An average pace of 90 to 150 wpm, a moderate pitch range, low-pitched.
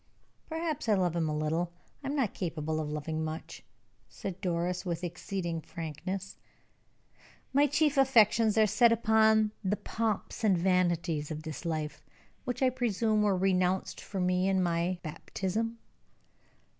No: average, 145 wpm; average, 4.6 semitones; medium, 185 Hz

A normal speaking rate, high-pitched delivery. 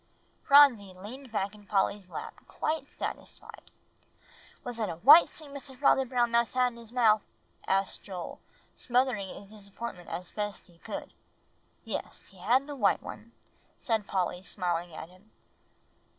Yes: average, 150 wpm; high, 215 Hz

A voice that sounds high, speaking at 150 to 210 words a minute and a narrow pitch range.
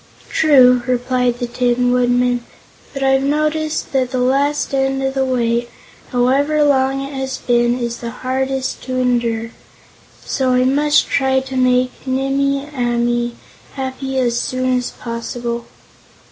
No: very high, 255 Hz; average, 140 wpm; narrow, 1.7 semitones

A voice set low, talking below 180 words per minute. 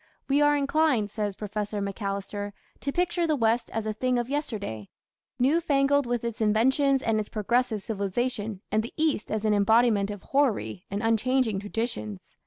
No: high, 225 Hz; average, 170 wpm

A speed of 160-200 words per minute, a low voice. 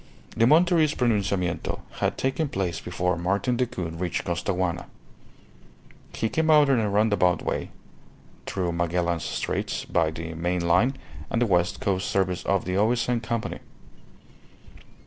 No: slow, 135 wpm; very low, 95 Hz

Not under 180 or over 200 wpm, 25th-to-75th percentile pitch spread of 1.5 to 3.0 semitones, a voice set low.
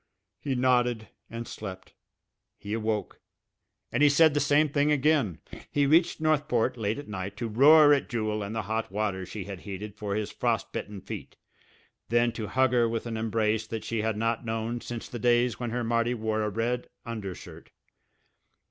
Yes: average, 185 wpm; average, 2.7 semitones; low, 115 Hz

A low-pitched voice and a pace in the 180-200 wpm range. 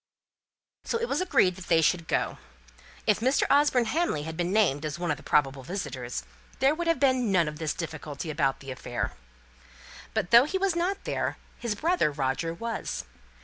No: medium, 180 Hz; average, 190 wpm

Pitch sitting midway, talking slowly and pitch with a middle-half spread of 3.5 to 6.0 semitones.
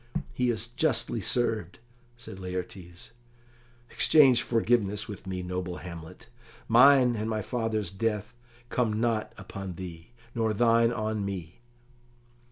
No: low, 110 Hz; slow, 120 wpm; average, 3.9 semitones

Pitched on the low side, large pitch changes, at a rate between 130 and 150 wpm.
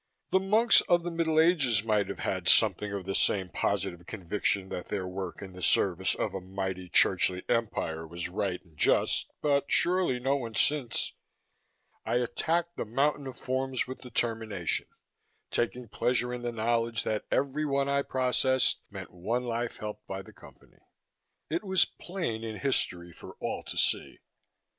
No: low, 115 Hz; wide, 6.1 semitones; average, 165 wpm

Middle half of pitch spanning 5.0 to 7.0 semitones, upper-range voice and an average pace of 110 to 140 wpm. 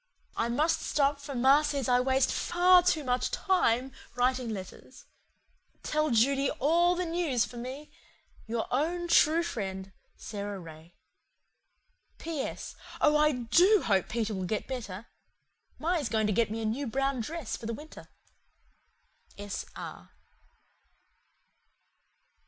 Yes: wide, 5.4 semitones; very high, 260 Hz; slow, 135 wpm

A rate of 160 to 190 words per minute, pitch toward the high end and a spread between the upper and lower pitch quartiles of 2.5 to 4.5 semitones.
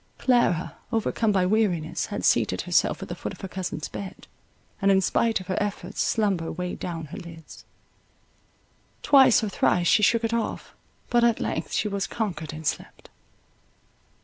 Yes: average, 170 wpm; high, 195 Hz; average, 4.1 semitones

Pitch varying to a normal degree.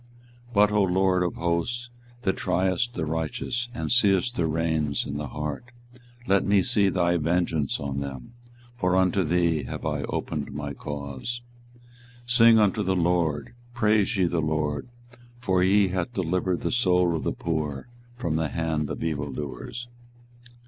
Yes: average, 4.3 semitones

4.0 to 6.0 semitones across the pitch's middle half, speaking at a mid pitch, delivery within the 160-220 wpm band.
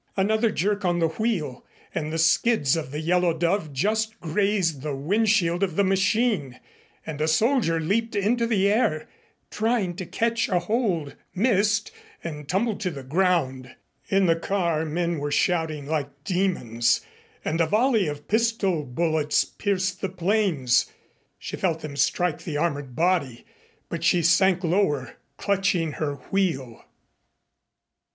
No: average, 4.7 semitones; medium, 175 Hz; average, 145 wpm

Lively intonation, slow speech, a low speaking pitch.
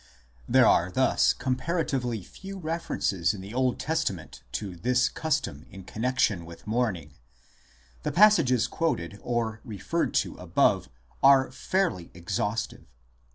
Yes: wide, 5.9 semitones; slow, 125 wpm; low, 120 Hz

